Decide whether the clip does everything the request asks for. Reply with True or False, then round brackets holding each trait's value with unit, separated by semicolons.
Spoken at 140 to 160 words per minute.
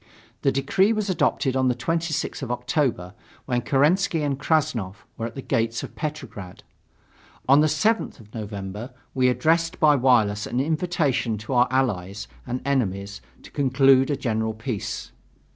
True (155 wpm)